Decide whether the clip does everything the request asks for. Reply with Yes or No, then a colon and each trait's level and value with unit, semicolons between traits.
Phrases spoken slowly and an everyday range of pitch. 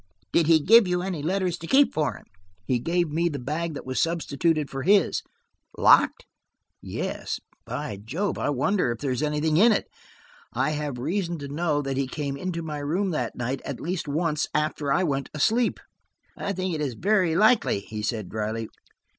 No: average, 190 wpm; average, 4.4 semitones